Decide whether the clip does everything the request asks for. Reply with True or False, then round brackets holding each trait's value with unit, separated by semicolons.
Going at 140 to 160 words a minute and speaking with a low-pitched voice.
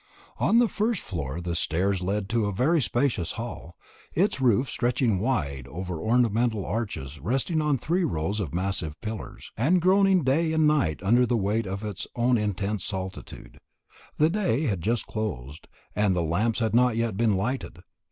False (170 wpm; 110 Hz)